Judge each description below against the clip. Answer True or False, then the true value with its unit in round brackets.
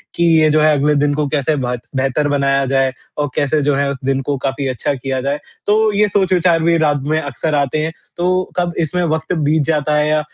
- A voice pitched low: False (145 Hz)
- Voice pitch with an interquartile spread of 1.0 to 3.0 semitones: True (2.6 semitones)